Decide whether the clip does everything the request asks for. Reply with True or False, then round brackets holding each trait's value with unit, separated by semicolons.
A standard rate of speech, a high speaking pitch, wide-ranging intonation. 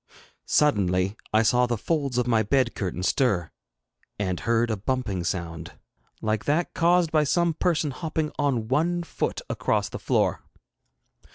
False (150 wpm; 125 Hz; 7.0 semitones)